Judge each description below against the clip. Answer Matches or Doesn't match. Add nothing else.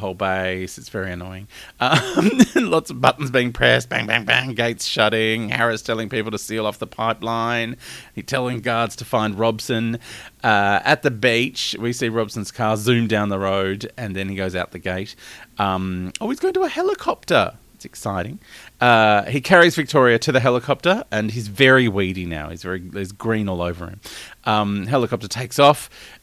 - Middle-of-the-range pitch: Doesn't match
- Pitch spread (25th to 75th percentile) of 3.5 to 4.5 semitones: Matches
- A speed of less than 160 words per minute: Doesn't match